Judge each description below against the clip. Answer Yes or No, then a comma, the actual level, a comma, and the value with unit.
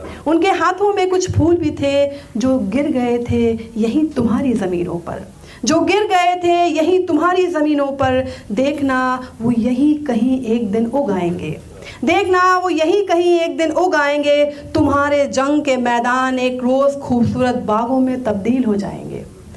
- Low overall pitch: No, very high, 275 Hz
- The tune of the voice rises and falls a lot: No, average, 4.9 semitones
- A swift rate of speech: No, average, 150 wpm